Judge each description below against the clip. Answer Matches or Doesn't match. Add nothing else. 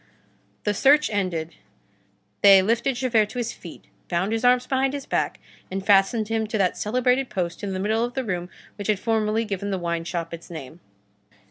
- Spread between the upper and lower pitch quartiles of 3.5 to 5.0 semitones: Matches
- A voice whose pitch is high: Matches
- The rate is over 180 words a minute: Matches